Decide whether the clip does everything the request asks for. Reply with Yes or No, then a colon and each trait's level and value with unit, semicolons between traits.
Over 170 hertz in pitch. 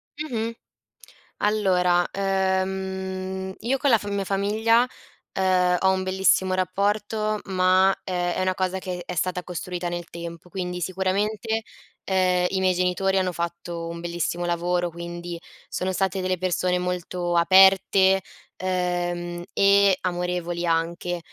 Yes: medium, 185 Hz